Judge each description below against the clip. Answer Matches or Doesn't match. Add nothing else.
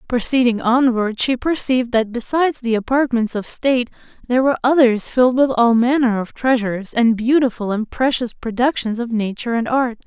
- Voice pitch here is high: Matches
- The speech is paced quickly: Doesn't match